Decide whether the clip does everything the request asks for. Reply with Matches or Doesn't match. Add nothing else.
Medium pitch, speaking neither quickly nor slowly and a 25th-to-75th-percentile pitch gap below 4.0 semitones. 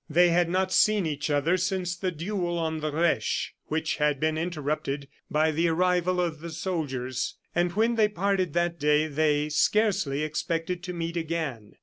Matches